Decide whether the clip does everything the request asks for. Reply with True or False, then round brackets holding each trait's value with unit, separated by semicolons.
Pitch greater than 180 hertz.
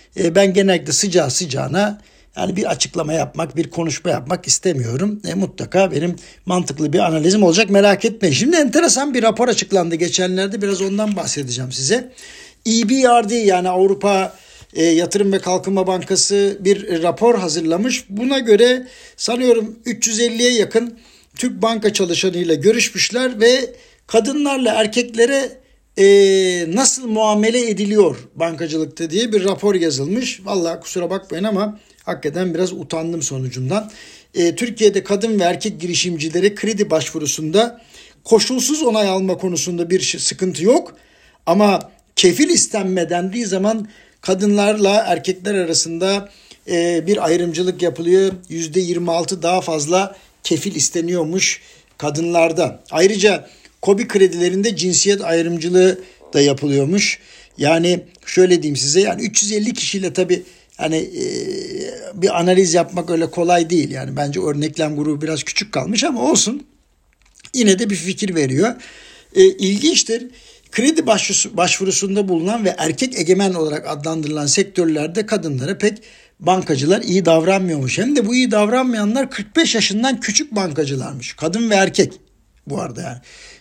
True (190 Hz)